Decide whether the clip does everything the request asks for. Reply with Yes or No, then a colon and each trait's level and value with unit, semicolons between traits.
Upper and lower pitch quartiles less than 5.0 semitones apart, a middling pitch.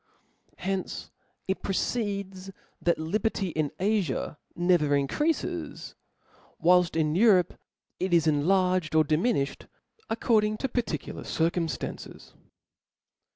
Yes: average, 4.3 semitones; medium, 180 Hz